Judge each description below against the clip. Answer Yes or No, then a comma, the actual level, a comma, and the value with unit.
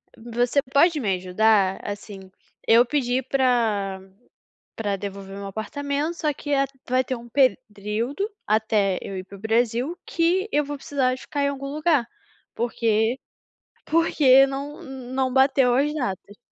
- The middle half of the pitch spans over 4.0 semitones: Yes, average, 4.9 semitones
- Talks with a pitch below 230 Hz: No, very high, 250 Hz